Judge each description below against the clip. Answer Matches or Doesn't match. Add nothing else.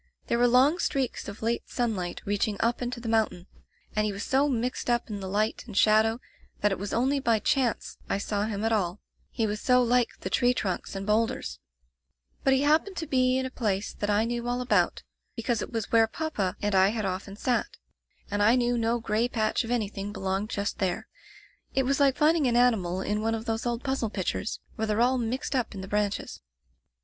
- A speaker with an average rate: Doesn't match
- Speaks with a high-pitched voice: Matches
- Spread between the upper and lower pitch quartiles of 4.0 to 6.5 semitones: Doesn't match